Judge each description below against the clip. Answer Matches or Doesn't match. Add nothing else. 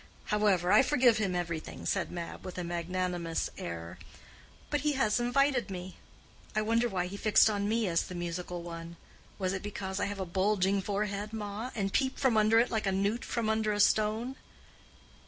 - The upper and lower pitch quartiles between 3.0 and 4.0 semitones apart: Matches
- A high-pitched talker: Matches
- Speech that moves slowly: Doesn't match